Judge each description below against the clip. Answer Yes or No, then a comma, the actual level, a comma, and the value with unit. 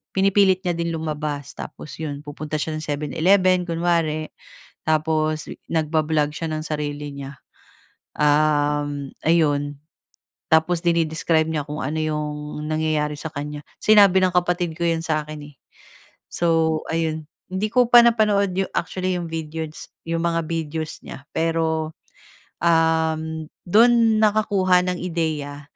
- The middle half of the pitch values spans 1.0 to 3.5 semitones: Yes, narrow, 2.5 semitones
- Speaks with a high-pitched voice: No, medium, 160 Hz